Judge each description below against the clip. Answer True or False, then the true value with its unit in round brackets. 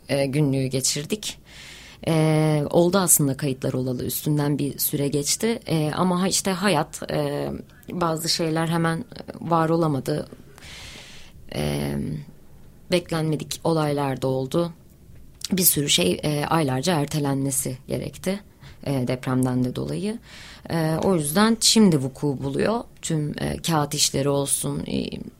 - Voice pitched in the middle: True (150 Hz)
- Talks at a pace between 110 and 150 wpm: False (95 wpm)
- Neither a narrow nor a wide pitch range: True (3.7 semitones)